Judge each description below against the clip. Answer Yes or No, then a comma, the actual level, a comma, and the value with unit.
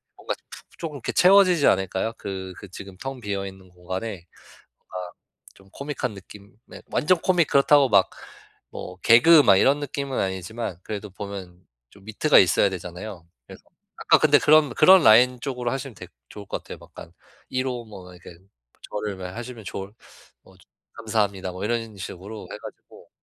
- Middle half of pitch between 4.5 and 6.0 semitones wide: Yes, wide, 5.4 semitones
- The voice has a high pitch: No, low, 105 Hz